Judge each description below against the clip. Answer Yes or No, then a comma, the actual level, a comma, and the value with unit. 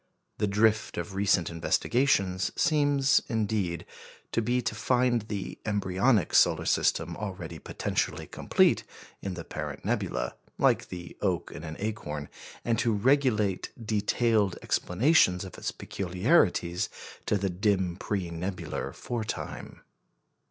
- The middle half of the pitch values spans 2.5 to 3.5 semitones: No, average, 4.2 semitones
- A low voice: Yes, low, 100 Hz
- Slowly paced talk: Yes, slow, 125 wpm